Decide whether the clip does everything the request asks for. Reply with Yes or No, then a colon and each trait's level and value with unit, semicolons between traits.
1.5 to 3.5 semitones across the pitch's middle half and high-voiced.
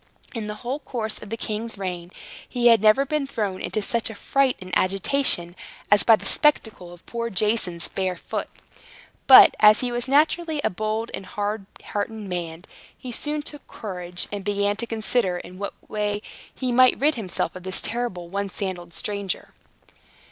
No: average, 4.2 semitones; high, 210 Hz